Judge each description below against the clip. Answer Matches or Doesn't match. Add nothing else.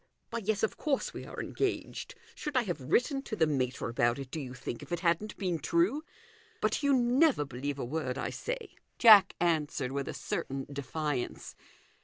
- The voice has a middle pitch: Matches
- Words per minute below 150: Doesn't match